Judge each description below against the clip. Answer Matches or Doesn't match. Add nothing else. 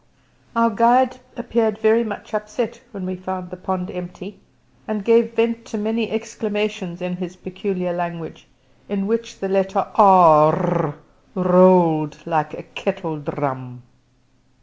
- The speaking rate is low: Matches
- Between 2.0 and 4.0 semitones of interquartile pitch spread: Matches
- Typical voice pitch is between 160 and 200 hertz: Matches